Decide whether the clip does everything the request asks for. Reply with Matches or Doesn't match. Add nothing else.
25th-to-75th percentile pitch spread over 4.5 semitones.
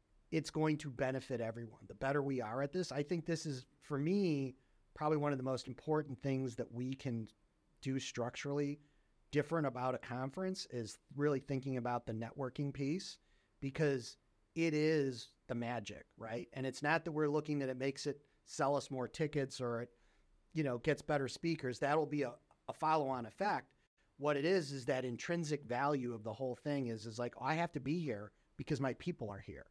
Doesn't match